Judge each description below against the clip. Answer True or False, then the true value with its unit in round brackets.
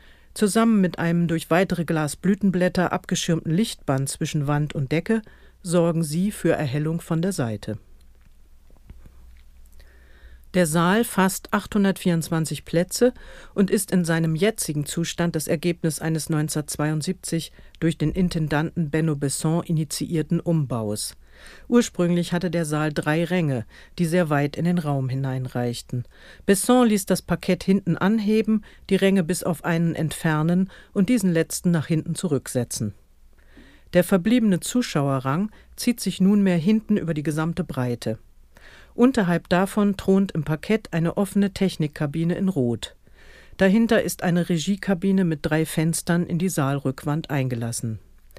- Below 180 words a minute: True (130 wpm)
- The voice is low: False (165 Hz)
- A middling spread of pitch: True (4.5 semitones)